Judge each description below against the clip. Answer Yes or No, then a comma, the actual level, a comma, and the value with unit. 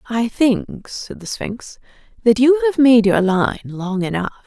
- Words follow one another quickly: No, average, 175 wpm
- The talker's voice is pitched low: No, high, 230 Hz